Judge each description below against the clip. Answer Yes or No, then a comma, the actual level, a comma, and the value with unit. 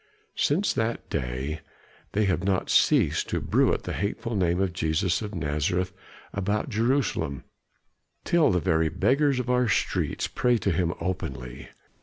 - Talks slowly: No, average, 145 wpm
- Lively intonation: Yes, wide, 6.0 semitones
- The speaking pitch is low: Yes, very low, 95 Hz